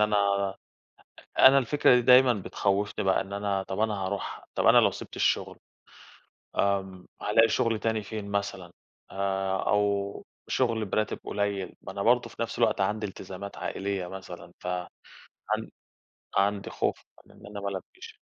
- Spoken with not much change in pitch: Yes, narrow, 2.0 semitones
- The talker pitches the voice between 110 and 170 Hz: No, low, 100 Hz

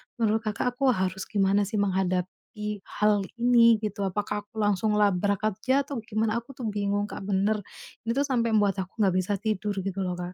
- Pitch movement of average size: No, narrow, 2.3 semitones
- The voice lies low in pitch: No, high, 210 Hz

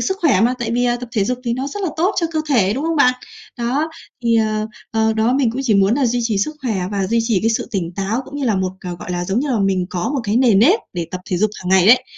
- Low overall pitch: No, high, 230 Hz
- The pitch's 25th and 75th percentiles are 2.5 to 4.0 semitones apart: No, average, 4.6 semitones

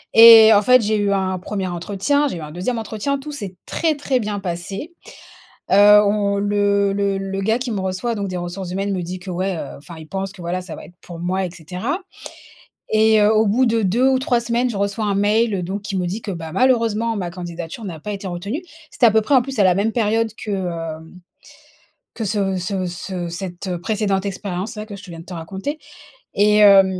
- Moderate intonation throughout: Yes, average, 3.2 semitones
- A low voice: No, high, 200 Hz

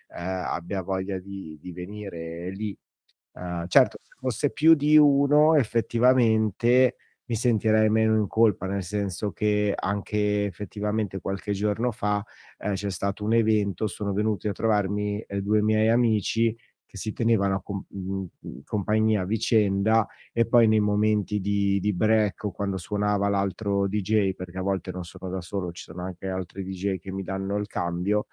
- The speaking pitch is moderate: No, low, 105 Hz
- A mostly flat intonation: Yes, narrow, 2.2 semitones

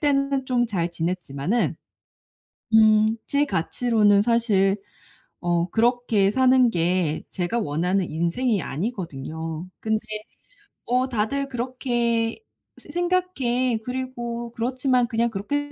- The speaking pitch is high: Yes, high, 230 Hz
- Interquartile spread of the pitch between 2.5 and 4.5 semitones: No, average, 5.3 semitones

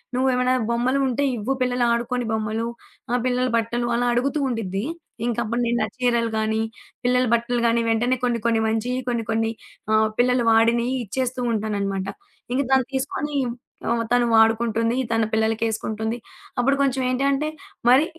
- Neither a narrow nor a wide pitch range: No, narrow, 2.0 semitones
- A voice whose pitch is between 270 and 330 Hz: No, high, 235 Hz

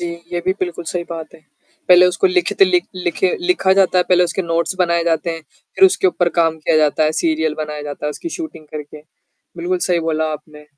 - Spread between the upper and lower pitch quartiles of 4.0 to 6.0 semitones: No, average, 2.7 semitones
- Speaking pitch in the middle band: Yes, medium, 170 Hz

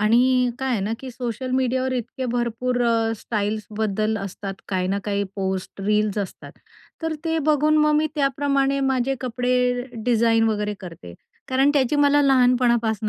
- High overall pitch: Yes, high, 245 Hz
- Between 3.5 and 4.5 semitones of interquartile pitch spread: Yes, average, 3.8 semitones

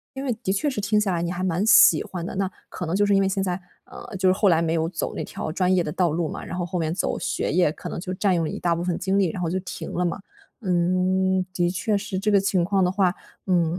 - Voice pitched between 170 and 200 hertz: Yes, medium, 185 Hz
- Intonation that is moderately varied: No, narrow, 2.1 semitones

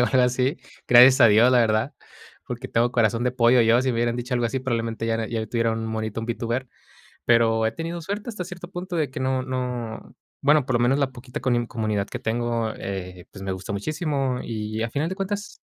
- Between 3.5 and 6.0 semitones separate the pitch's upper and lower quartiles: No, average, 2.8 semitones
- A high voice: No, low, 120 Hz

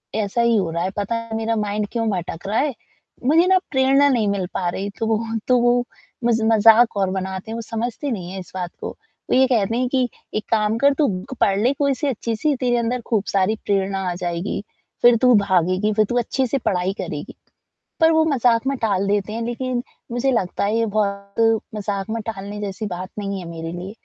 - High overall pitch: Yes, high, 220 Hz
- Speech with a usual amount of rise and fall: Yes, average, 3.7 semitones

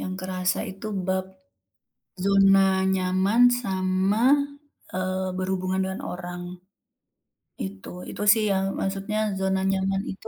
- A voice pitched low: No, high, 190 Hz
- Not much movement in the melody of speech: Yes, narrow, 0.8 semitones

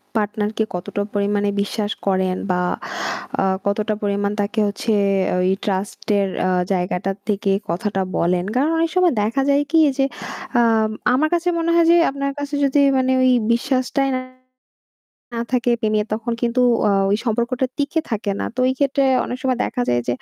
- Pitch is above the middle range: Yes, high, 220 Hz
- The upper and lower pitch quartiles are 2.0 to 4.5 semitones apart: No, average, 4.9 semitones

